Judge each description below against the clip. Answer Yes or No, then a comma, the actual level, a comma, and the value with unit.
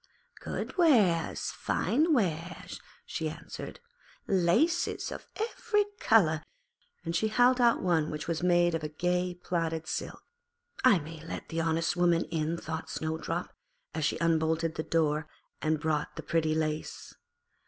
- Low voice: No, medium, 165 Hz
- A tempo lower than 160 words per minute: Yes, average, 140 wpm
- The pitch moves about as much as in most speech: No, narrow, 2.3 semitones